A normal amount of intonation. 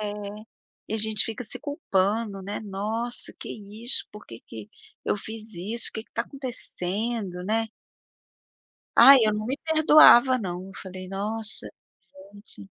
Yes: average, 3.2 semitones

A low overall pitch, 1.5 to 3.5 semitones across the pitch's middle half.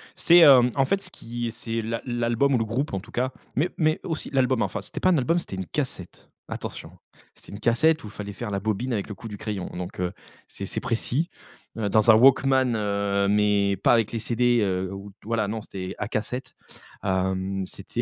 No: low, 115 Hz; average, 4.2 semitones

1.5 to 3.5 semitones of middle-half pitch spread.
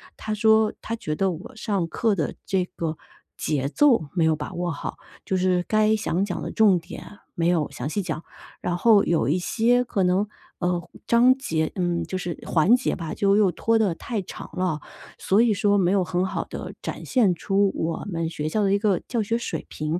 No: average, 4.2 semitones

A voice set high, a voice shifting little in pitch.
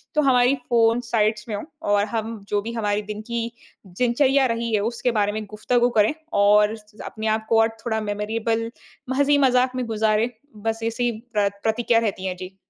Yes: high, 225 Hz; narrow, 2.2 semitones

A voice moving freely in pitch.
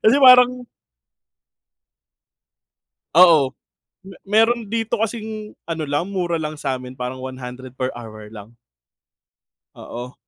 Yes: wide, 9.0 semitones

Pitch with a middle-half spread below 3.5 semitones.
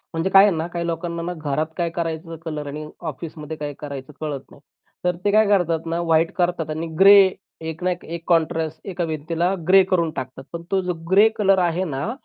Yes: narrow, 2.4 semitones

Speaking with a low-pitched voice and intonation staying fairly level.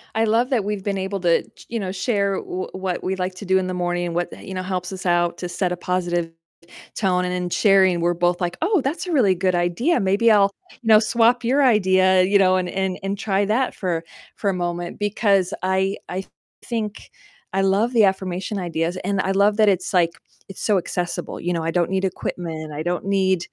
No: high, 190 Hz; narrow, 2.3 semitones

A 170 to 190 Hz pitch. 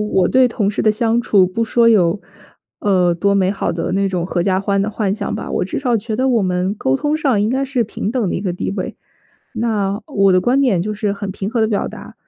No: high, 205 Hz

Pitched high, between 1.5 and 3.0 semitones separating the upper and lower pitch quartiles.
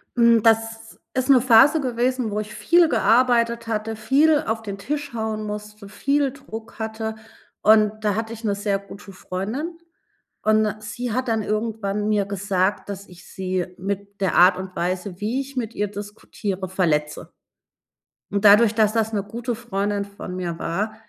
Yes: high, 215 Hz; narrow, 2.6 semitones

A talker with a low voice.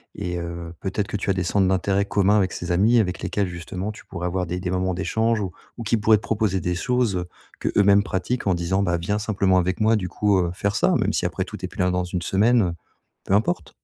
Yes: very low, 95 Hz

